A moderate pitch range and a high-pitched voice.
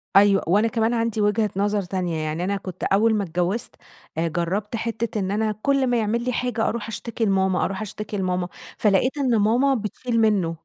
Yes: average, 3.2 semitones; high, 210 Hz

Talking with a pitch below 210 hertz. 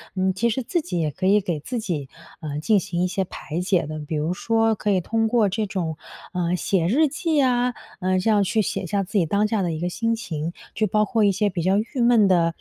Yes: high, 195 Hz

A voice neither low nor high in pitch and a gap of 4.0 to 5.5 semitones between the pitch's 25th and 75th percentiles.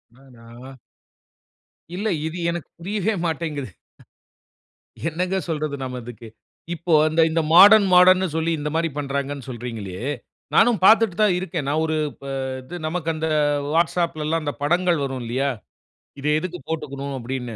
Yes: medium, 155 Hz; average, 4.5 semitones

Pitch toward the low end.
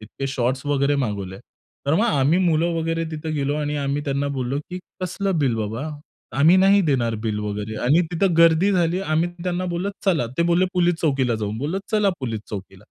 No: medium, 150 Hz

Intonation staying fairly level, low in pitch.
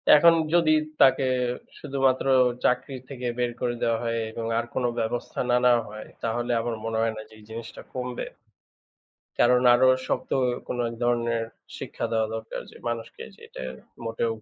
Yes: narrow, 1.8 semitones; low, 120 Hz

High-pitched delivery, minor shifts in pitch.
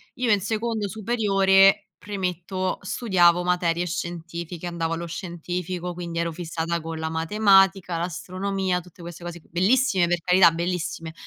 No: medium, 180 Hz; narrow, 2.2 semitones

